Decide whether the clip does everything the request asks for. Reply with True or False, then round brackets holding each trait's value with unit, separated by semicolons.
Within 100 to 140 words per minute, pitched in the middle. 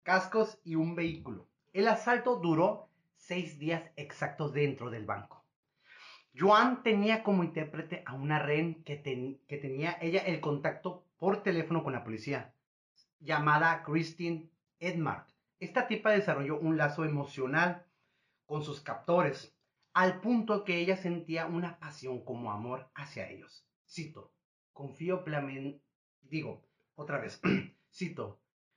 True (125 wpm; 165 Hz)